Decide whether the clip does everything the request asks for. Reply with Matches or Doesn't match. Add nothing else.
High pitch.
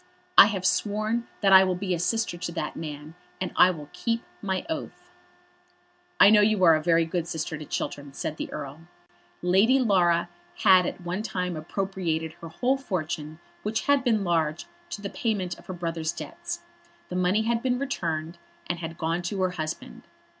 Doesn't match